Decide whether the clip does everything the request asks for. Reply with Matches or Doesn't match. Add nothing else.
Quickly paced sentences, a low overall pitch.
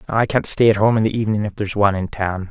Matches